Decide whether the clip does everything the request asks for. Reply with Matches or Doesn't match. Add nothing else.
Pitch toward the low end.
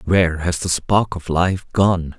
Matches